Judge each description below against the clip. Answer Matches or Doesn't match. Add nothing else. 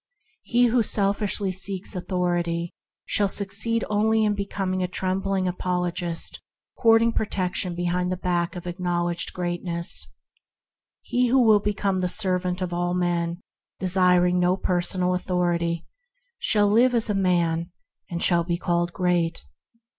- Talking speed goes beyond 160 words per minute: Doesn't match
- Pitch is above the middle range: Doesn't match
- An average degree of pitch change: Doesn't match